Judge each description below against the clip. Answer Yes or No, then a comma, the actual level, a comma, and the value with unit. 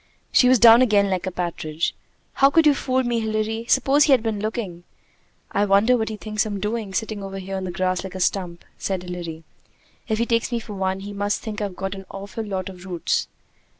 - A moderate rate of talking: No, fast, 225 wpm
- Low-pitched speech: No, high, 205 Hz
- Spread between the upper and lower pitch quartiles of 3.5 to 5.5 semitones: No, average, 3.1 semitones